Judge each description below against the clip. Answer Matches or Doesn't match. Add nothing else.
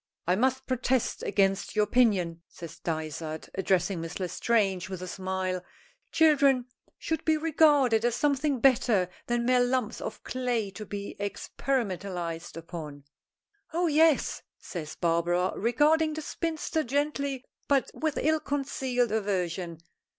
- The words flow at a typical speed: Doesn't match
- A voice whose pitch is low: Doesn't match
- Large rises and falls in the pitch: Matches